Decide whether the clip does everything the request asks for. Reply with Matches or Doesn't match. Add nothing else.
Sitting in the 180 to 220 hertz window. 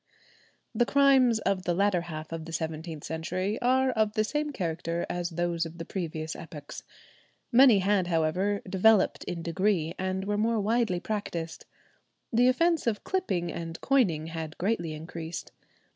Matches